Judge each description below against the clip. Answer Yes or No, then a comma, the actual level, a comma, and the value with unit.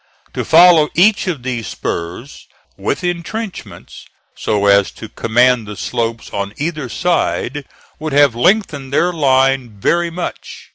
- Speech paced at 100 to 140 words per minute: Yes, slow, 135 wpm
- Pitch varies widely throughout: Yes, wide, 6.9 semitones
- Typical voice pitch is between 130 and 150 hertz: Yes, low, 135 Hz